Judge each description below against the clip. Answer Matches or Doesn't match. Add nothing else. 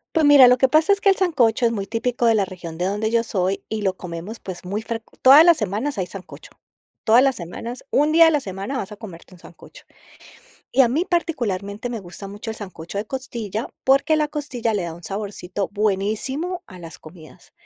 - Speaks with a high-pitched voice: Matches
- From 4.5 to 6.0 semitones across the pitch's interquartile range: Matches